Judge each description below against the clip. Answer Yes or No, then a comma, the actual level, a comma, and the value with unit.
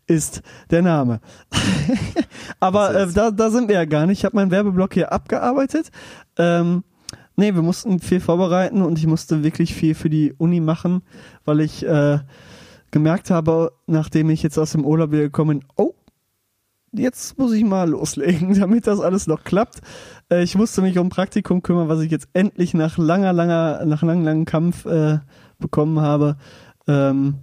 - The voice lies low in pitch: No, medium, 170 Hz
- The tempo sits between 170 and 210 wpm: Yes, average, 175 wpm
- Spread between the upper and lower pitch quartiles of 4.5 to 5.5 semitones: No, average, 3.4 semitones